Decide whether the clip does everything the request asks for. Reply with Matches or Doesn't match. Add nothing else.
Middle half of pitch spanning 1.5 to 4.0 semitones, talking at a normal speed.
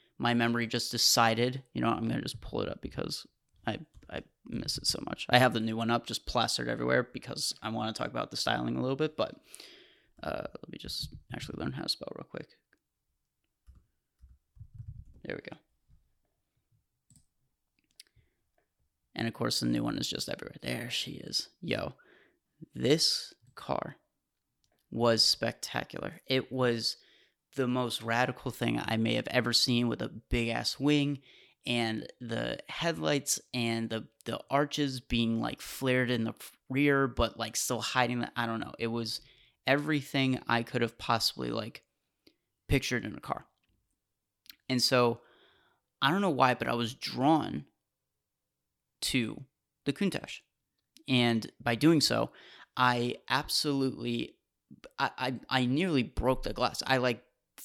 Matches